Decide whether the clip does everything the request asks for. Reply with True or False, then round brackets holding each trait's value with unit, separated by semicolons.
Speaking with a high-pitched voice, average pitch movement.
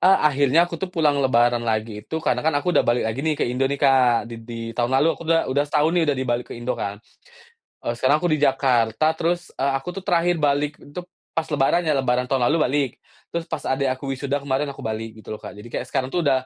False (135 Hz; 4.1 semitones)